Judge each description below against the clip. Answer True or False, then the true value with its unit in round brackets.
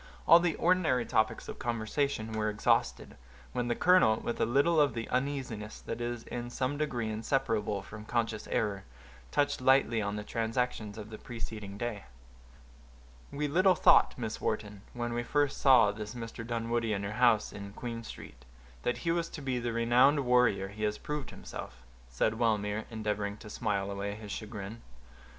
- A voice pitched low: True (115 Hz)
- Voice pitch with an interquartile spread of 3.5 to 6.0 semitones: False (3.1 semitones)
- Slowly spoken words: False (175 wpm)